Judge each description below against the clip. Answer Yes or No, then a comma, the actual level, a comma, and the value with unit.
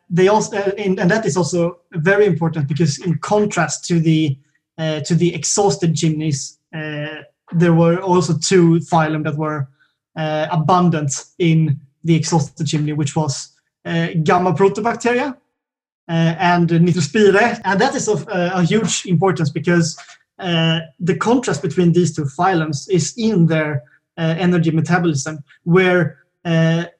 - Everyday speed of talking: Yes, average, 145 wpm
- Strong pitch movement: No, average, 3.0 semitones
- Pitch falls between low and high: Yes, medium, 170 Hz